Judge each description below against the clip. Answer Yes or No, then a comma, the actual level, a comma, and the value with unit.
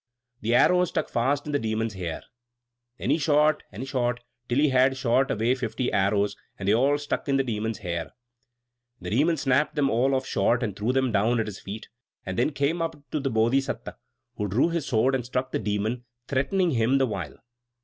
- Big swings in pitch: No, average, 4.1 semitones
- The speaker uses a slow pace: No, average, 200 wpm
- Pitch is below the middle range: Yes, low, 125 Hz